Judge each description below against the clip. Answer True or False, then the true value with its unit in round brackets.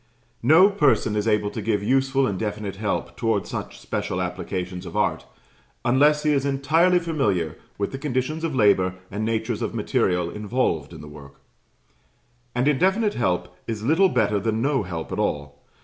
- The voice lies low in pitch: True (115 Hz)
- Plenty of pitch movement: True (6.1 semitones)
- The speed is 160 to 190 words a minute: True (170 wpm)